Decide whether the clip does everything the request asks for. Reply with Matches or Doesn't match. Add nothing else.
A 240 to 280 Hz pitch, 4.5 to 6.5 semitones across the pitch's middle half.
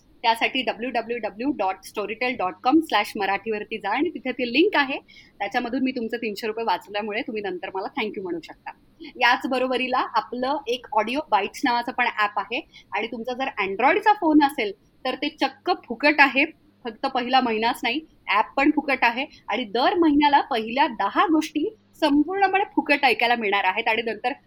Matches